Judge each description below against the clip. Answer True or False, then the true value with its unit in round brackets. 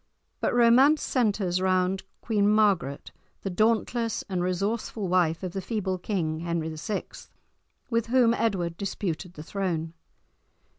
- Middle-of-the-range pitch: False (195 Hz)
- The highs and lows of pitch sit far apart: False (4.0 semitones)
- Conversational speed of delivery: False (130 wpm)